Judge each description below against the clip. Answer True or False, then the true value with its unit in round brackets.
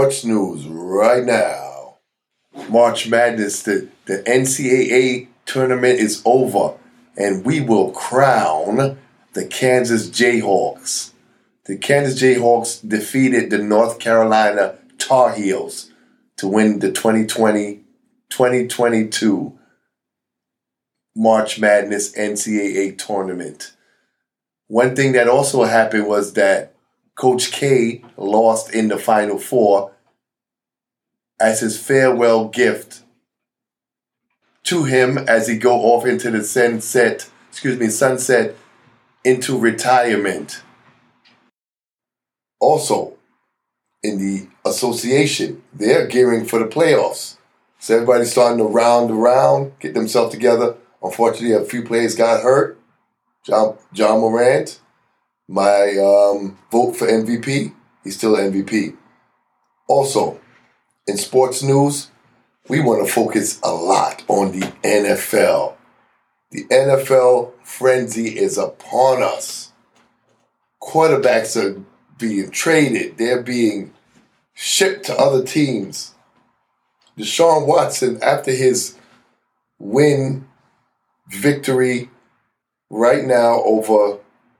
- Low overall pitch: True (115 Hz)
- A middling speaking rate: False (100 wpm)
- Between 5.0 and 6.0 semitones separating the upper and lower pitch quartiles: False (3.2 semitones)